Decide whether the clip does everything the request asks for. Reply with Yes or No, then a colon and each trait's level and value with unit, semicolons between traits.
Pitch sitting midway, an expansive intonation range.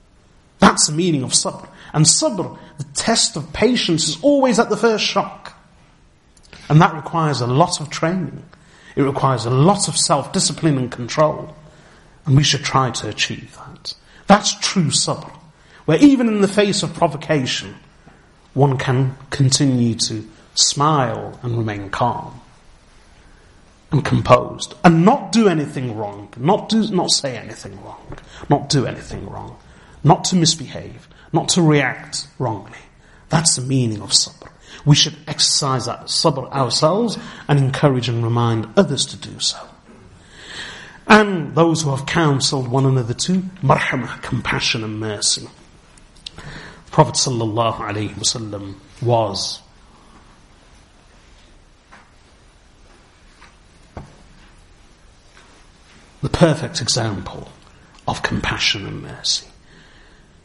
Yes: medium, 145 Hz; wide, 5.7 semitones